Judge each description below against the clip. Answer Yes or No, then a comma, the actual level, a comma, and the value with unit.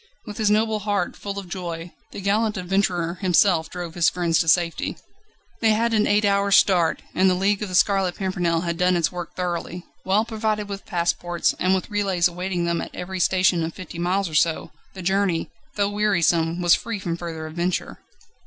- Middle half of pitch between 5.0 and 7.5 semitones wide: No, average, 2.7 semitones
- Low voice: No, medium, 185 Hz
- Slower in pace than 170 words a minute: No, average, 195 wpm